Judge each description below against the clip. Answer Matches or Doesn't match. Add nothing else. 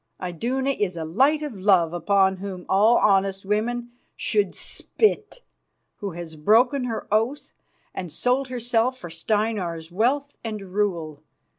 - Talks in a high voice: Matches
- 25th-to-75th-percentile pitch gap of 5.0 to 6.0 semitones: Matches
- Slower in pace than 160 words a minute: Matches